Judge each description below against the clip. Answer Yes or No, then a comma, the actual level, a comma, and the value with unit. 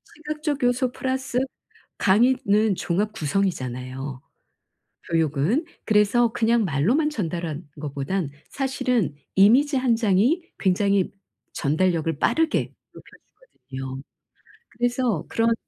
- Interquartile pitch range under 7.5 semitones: No, wide, 7.8 semitones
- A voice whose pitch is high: Yes, high, 205 Hz